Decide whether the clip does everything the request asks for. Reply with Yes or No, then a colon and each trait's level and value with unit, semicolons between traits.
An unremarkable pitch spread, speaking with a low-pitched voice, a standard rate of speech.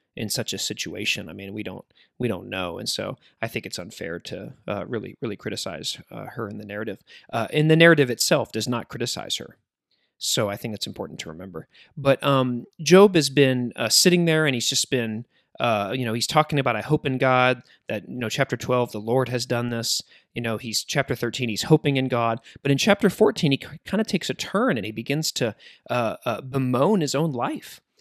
No: average, 4.1 semitones; low, 125 Hz; fast, 225 wpm